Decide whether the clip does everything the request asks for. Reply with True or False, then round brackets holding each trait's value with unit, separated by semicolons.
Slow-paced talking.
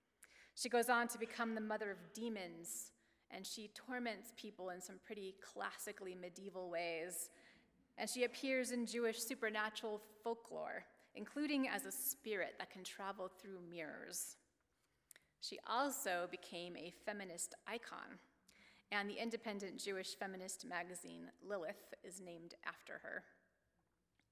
True (130 wpm)